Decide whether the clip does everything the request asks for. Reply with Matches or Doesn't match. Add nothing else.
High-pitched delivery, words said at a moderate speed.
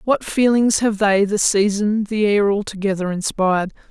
Matches